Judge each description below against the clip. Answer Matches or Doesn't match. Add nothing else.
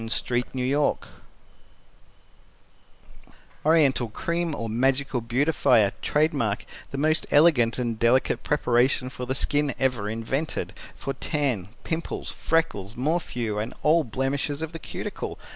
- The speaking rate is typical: Doesn't match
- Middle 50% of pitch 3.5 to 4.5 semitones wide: Matches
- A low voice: Matches